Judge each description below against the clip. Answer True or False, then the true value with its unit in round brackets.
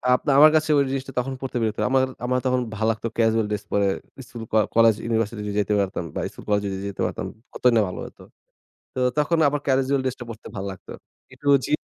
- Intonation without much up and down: False (4.1 semitones)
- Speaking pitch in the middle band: False (115 Hz)